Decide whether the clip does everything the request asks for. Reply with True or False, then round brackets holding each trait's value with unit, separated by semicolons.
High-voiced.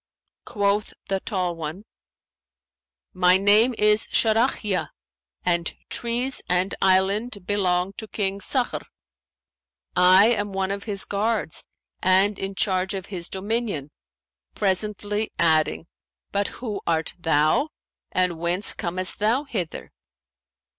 True (195 Hz)